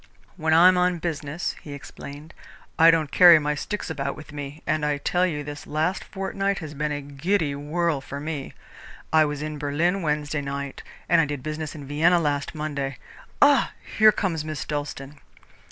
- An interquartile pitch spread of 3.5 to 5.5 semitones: No, average, 2.7 semitones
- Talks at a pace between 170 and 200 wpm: Yes, average, 185 wpm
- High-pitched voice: No, medium, 150 Hz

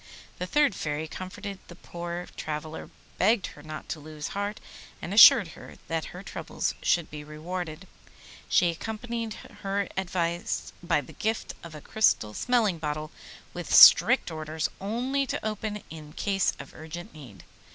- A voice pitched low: No, medium, 175 Hz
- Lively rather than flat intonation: No, average, 4.7 semitones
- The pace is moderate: Yes, average, 155 wpm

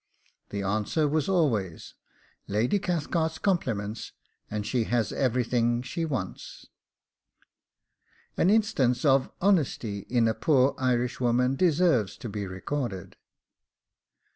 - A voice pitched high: No, low, 125 Hz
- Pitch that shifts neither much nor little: No, wide, 6.5 semitones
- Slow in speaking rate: Yes, slow, 105 wpm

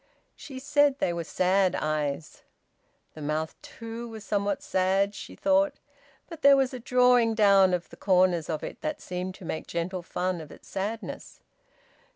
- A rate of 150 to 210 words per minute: Yes, average, 170 wpm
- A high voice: Yes, high, 195 Hz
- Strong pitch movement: Yes, wide, 5.9 semitones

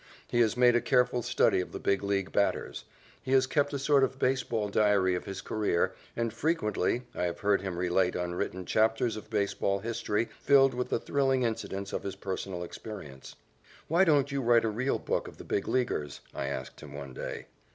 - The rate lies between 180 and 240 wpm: Yes, average, 200 wpm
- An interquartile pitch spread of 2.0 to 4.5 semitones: No, average, 5.0 semitones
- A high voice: No, low, 110 Hz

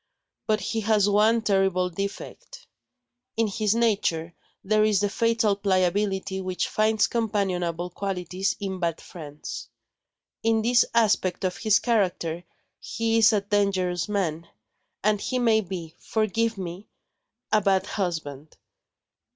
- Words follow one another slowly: Yes, slow, 125 wpm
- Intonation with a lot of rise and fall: No, average, 3.2 semitones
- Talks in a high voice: Yes, high, 200 Hz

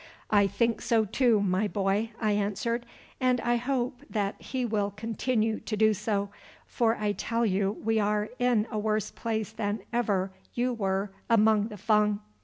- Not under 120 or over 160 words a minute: No, average, 170 wpm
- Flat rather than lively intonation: Yes, narrow, 2.2 semitones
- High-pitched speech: Yes, high, 215 Hz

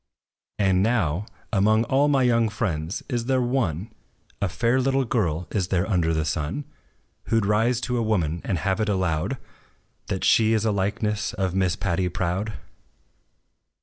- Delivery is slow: No, average, 165 wpm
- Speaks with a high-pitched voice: No, low, 105 Hz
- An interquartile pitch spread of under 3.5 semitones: No, average, 4.3 semitones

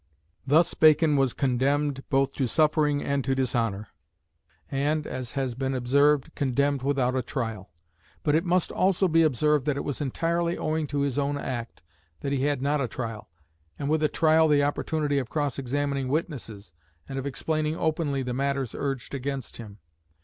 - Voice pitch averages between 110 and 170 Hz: Yes, medium, 140 Hz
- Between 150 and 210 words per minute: Yes, average, 175 wpm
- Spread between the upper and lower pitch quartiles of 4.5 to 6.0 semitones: No, narrow, 2.5 semitones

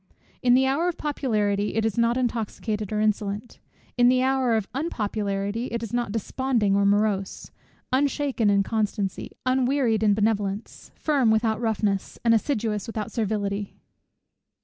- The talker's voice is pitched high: Yes, high, 220 Hz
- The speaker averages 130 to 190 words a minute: Yes, average, 145 wpm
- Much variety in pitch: No, average, 3.3 semitones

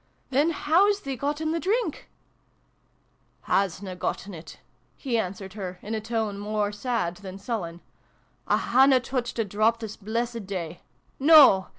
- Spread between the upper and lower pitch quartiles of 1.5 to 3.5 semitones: No, average, 5.2 semitones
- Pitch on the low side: No, high, 220 Hz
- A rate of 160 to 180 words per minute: Yes, average, 170 wpm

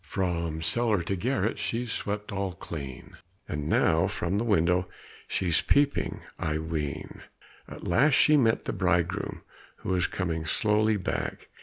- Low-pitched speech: Yes, very low, 95 Hz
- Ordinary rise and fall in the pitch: Yes, average, 4.4 semitones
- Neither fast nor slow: Yes, average, 145 wpm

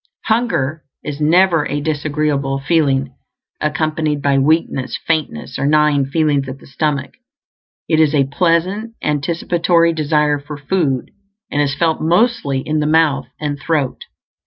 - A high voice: No, medium, 150 Hz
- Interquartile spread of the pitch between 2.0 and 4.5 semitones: Yes, narrow, 2.6 semitones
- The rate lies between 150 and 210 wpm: No, slow, 135 wpm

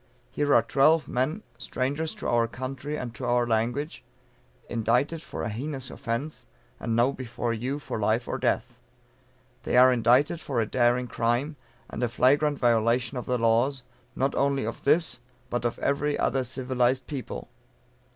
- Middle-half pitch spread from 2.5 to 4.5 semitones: Yes, average, 2.9 semitones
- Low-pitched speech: Yes, low, 125 Hz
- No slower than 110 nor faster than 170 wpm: Yes, average, 160 wpm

